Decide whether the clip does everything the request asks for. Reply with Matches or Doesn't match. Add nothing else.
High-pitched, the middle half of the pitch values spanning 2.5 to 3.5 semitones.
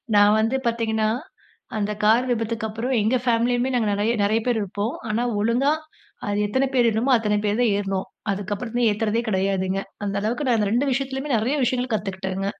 Matches